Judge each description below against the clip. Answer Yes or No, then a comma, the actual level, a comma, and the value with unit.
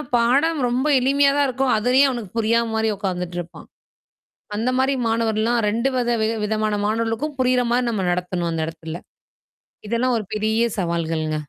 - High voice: Yes, high, 225 Hz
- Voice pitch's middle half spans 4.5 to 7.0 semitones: Yes, average, 5.0 semitones